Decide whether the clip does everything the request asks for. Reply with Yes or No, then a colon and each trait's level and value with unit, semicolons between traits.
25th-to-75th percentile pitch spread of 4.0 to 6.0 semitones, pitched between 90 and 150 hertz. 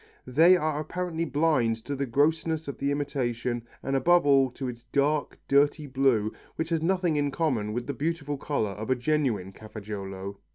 Yes: average, 4.6 semitones; medium, 140 Hz